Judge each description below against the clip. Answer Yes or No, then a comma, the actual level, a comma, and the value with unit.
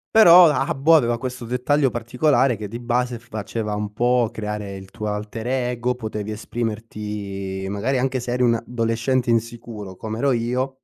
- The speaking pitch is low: Yes, low, 115 Hz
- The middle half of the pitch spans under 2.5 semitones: No, average, 2.8 semitones